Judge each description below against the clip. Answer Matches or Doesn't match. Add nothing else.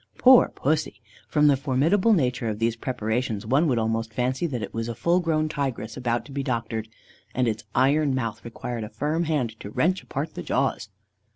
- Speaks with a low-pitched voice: Matches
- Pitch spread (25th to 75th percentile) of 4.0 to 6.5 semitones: Matches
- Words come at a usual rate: Matches